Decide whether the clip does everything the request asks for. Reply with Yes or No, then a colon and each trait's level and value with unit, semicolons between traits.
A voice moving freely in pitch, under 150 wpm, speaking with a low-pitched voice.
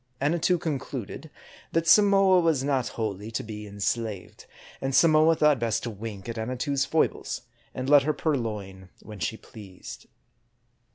Yes: wide, 6.3 semitones; average, 140 wpm; low, 130 Hz